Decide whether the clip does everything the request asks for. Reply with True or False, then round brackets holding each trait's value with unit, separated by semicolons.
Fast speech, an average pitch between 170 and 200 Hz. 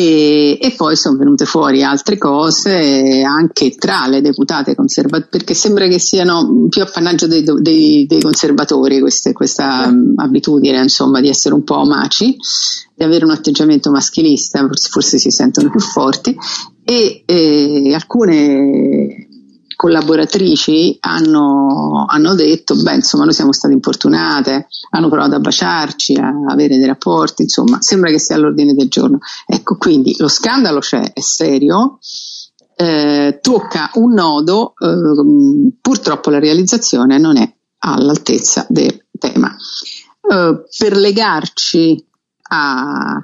False (135 wpm; 185 Hz)